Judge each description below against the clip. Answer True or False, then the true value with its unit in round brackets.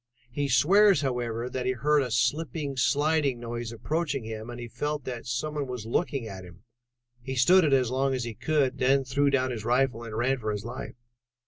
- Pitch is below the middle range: True (130 Hz)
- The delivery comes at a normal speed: False (215 wpm)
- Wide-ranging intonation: False (3.3 semitones)